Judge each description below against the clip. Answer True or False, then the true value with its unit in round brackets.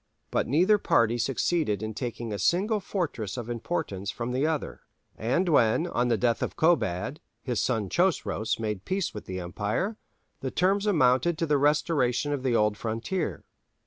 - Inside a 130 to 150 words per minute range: False (170 wpm)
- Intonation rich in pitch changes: True (7.4 semitones)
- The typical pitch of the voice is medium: False (125 Hz)